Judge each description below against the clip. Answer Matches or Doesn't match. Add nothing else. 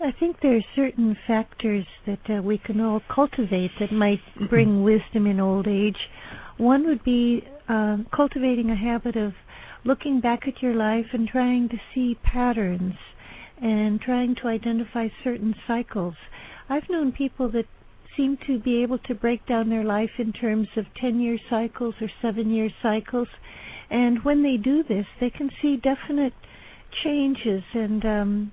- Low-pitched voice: Doesn't match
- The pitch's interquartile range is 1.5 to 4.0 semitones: Matches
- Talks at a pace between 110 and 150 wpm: Doesn't match